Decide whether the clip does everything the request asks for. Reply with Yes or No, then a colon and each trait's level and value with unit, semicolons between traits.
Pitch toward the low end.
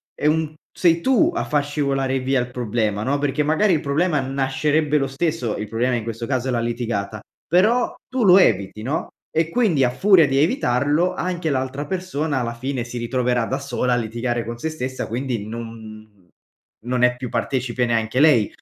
Yes: low, 130 Hz